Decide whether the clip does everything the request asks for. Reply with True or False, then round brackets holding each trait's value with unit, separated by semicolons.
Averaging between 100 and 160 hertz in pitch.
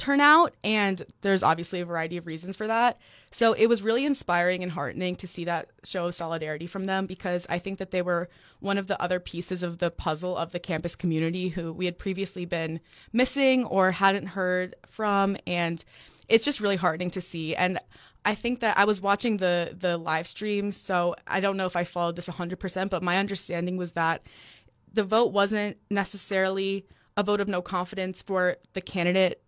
False (185 Hz)